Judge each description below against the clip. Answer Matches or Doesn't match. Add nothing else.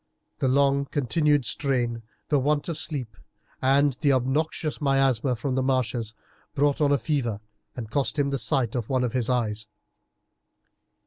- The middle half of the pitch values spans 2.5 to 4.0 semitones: Matches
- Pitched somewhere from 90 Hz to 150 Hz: Matches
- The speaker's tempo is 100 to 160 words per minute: Matches